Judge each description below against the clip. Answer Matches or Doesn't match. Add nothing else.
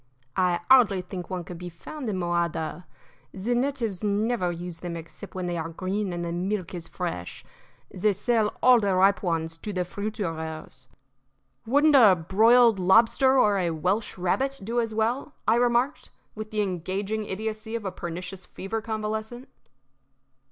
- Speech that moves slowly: Doesn't match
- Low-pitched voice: Doesn't match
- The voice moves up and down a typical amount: Matches